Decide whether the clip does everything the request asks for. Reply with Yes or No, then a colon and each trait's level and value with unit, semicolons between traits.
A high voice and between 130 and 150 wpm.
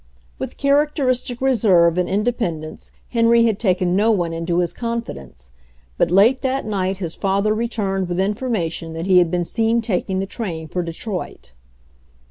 No: high, 195 Hz; average, 165 wpm